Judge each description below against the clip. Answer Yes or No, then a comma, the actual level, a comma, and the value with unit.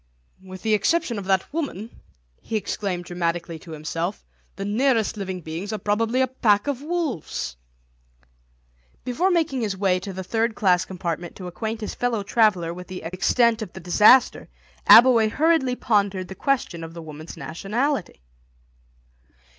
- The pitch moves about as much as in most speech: Yes, average, 5.0 semitones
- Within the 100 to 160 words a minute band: Yes, average, 155 wpm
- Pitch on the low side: No, high, 205 Hz